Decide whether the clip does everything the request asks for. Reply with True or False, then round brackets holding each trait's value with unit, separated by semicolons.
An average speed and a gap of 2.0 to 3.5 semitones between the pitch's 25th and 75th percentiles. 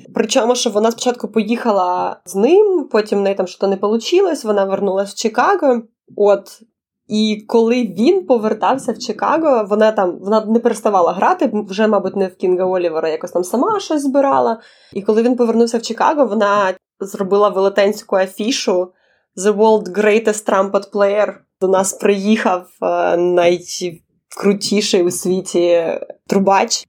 True (145 wpm; 3.2 semitones)